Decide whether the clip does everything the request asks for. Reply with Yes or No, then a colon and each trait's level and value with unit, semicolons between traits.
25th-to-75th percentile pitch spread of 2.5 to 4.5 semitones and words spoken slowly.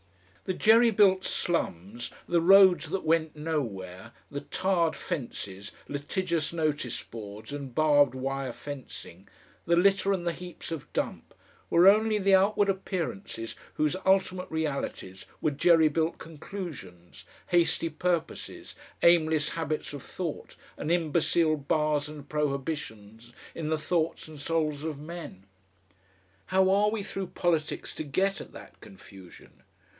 Yes: average, 4.1 semitones; slow, 130 wpm